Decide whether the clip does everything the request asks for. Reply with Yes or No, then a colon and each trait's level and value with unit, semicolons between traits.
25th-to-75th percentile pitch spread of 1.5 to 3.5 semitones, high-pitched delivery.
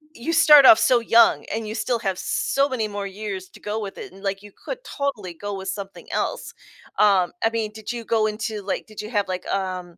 Yes: average, 2.8 semitones; high, 210 Hz